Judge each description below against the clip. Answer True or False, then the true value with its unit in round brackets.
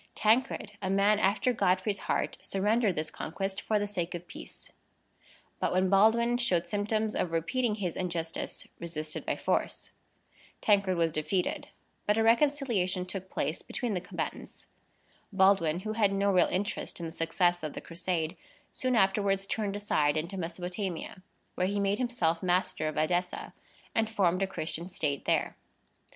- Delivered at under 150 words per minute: False (155 wpm)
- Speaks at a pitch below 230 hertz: True (190 Hz)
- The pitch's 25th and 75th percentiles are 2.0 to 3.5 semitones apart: True (3.2 semitones)